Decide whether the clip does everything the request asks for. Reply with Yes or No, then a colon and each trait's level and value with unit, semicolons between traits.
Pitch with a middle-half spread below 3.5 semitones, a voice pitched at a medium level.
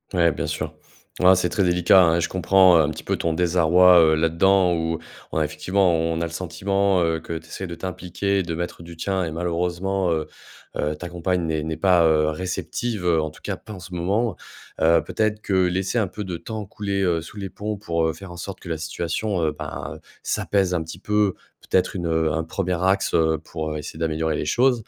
No: average, 2.8 semitones; very low, 85 Hz